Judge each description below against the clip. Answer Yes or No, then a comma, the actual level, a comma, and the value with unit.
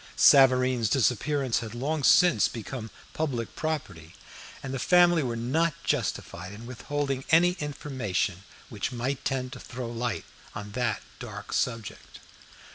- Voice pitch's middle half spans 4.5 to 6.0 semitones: No, average, 4.0 semitones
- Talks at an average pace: No, slow, 130 wpm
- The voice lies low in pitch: Yes, low, 125 Hz